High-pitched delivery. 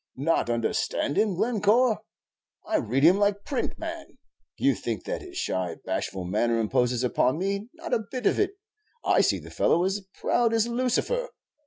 Yes: high, 200 Hz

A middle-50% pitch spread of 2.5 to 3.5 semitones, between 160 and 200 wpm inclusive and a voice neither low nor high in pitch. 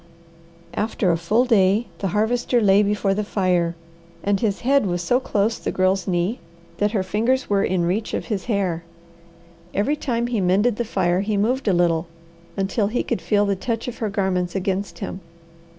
No: average, 3.2 semitones; average, 185 wpm; high, 200 Hz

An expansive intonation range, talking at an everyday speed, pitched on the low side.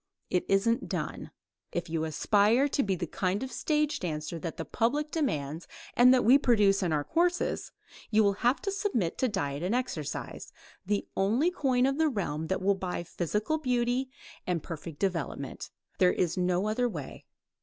No: wide, 6.7 semitones; average, 175 wpm; high, 205 Hz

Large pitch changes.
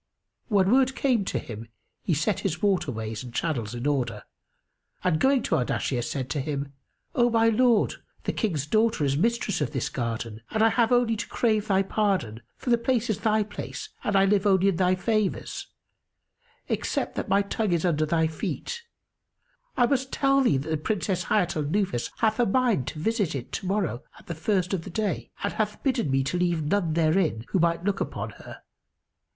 Yes: wide, 6.6 semitones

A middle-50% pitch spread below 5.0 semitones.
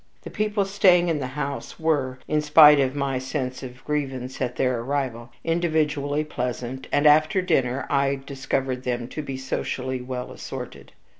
Yes: average, 2.8 semitones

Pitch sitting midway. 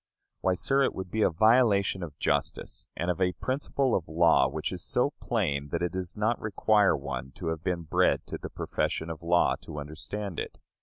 No: very low, 90 Hz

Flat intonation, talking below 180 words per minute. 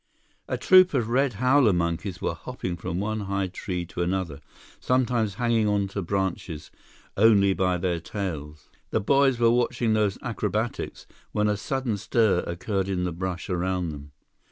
No: average, 4.2 semitones; average, 160 wpm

